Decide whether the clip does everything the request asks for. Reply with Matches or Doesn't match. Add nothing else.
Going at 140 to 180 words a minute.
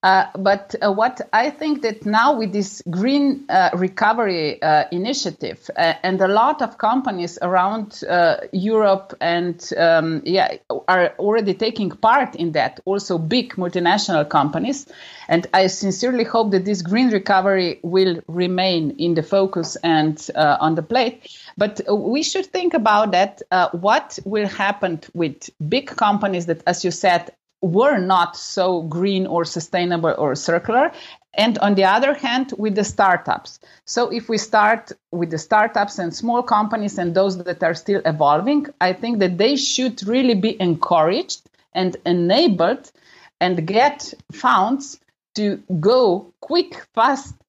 Matches